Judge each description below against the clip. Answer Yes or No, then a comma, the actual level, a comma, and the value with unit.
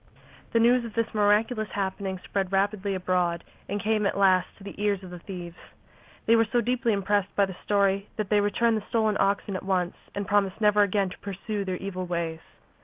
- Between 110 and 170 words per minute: No, fast, 205 wpm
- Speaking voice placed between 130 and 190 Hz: No, high, 200 Hz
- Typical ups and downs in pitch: No, narrow, 2.1 semitones